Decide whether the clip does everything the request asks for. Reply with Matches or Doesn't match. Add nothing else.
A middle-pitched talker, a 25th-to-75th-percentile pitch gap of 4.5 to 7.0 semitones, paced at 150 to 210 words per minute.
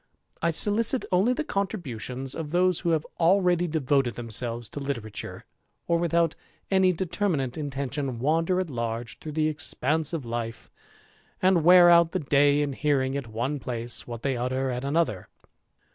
Matches